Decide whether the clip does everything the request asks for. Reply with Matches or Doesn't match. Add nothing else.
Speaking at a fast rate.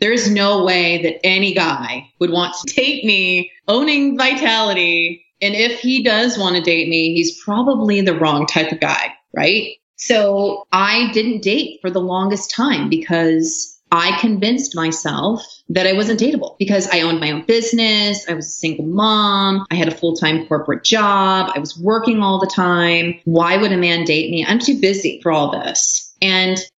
Doesn't match